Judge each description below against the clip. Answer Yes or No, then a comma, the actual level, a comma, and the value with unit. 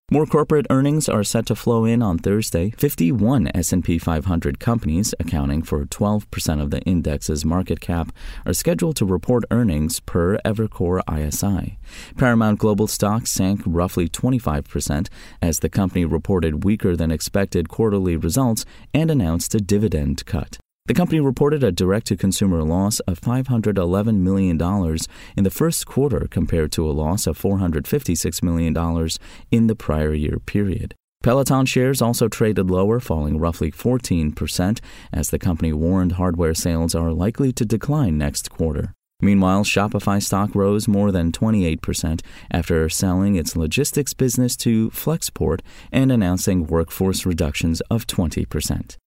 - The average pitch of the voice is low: Yes, very low, 95 Hz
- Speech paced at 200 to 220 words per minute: No, average, 145 wpm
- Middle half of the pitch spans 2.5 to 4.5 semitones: No, average, 5.3 semitones